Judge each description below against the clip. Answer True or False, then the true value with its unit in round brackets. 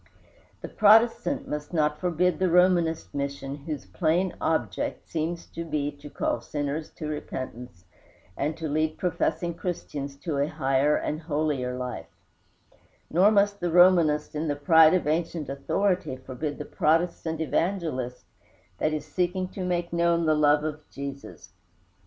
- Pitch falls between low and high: True (155 Hz)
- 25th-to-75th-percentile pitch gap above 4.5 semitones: False (3.2 semitones)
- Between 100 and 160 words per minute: True (145 wpm)